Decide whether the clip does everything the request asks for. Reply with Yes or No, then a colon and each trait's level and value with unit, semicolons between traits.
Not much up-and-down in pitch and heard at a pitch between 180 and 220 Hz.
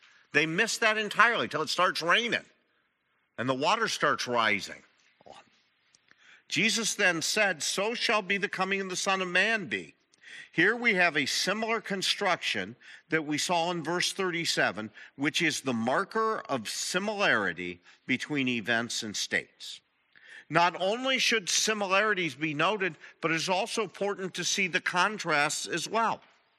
No: average, 4.8 semitones; medium, 185 Hz